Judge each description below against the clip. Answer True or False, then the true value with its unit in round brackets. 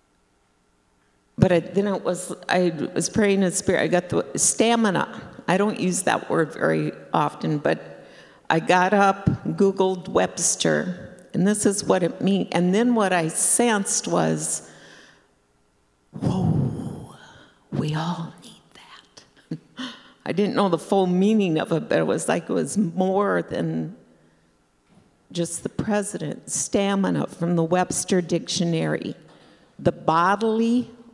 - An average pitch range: False (7.0 semitones)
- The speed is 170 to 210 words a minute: False (135 wpm)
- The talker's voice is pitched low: False (180 Hz)